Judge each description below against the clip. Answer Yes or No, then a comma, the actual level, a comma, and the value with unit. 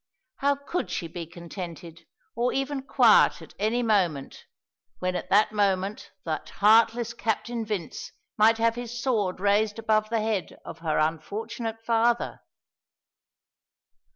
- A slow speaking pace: Yes, slow, 130 wpm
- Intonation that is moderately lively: Yes, average, 4.1 semitones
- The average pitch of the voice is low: No, high, 215 Hz